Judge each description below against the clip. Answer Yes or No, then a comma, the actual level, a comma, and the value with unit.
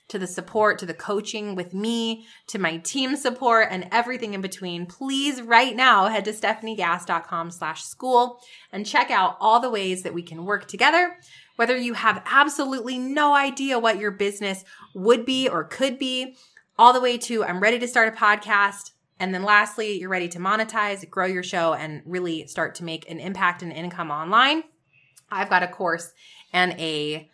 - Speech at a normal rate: Yes, average, 180 wpm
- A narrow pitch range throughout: No, average, 5.3 semitones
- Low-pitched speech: No, high, 205 Hz